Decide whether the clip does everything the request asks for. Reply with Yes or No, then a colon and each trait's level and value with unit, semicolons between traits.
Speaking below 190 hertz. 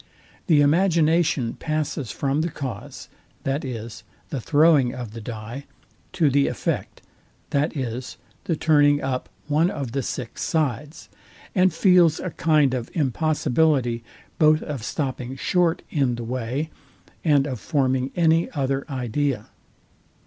Yes: medium, 140 Hz